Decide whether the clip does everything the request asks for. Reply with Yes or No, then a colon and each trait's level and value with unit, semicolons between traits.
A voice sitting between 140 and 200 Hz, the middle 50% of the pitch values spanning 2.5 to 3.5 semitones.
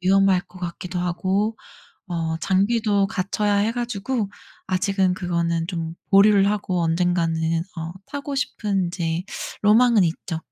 Yes: high, 190 Hz; average, 3.1 semitones